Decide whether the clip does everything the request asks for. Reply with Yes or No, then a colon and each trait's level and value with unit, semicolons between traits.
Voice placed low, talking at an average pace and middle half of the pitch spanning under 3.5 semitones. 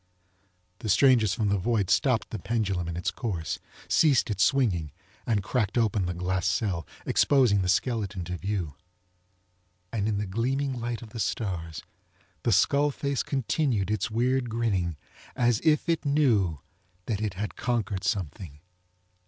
No: low, 110 Hz; average, 155 wpm; average, 4.6 semitones